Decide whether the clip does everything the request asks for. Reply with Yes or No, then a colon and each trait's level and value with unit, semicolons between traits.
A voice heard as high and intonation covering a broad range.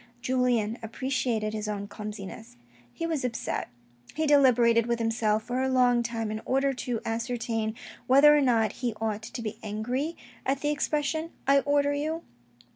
No: high, 240 Hz; average, 3.9 semitones